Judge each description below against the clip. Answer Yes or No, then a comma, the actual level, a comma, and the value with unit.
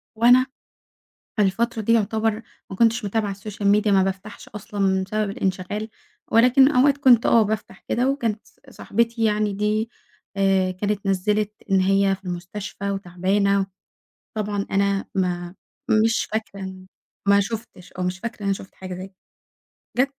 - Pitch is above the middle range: Yes, high, 205 Hz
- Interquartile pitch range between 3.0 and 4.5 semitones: No, narrow, 2.5 semitones